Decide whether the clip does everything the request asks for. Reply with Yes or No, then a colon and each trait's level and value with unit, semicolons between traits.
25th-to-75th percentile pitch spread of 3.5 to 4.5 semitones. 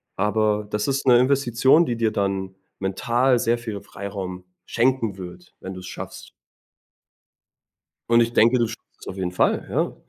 Yes: average, 3.9 semitones